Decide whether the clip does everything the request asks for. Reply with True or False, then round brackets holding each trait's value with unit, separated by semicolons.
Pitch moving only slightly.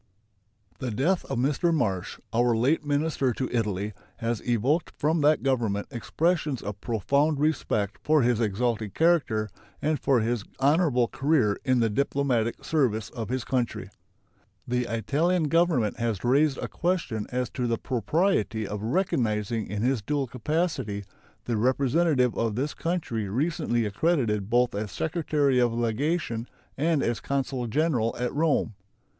False (5.0 semitones)